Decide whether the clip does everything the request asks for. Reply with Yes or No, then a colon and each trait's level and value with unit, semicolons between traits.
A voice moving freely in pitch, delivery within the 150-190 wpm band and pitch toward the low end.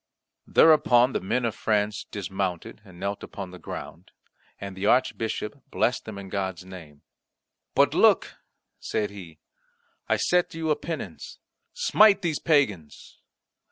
No: wide, 6.8 semitones; slow, 135 wpm; low, 105 Hz